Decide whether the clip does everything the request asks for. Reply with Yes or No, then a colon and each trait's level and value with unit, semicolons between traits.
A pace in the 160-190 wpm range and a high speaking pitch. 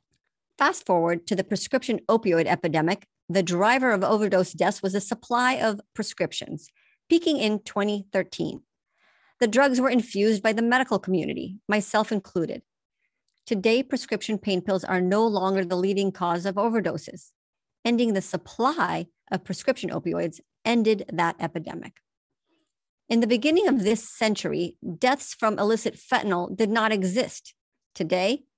No: slow, 135 wpm; high, 210 Hz